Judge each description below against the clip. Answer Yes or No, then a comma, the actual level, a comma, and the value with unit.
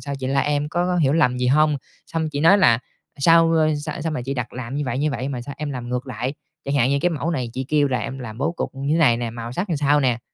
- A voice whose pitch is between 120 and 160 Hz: Yes, medium, 140 Hz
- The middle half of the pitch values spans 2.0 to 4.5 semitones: Yes, average, 3.5 semitones